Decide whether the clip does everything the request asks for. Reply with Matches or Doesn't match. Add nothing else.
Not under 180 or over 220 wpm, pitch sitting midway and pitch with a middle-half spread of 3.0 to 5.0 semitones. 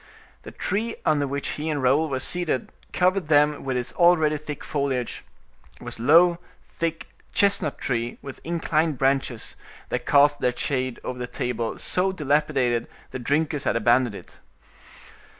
Doesn't match